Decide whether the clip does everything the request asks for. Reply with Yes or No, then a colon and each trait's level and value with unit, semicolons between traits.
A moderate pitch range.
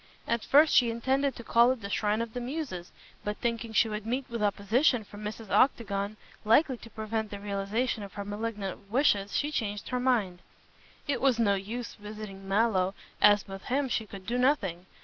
Yes: average, 3.4 semitones